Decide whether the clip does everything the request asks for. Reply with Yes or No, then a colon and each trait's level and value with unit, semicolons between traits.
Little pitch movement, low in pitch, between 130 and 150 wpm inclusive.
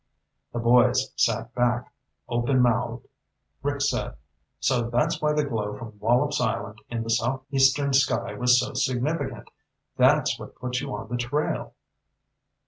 Yes: narrow, 2.1 semitones; low, 125 Hz; average, 140 wpm